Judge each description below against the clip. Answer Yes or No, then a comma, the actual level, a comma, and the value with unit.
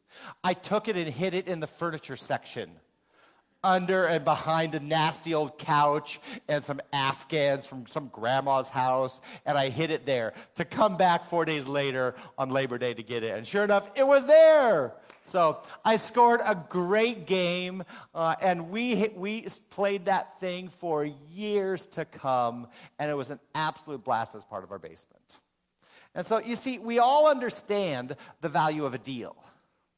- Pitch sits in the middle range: Yes, medium, 160 Hz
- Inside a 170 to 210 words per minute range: Yes, average, 175 wpm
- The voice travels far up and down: Yes, wide, 5.8 semitones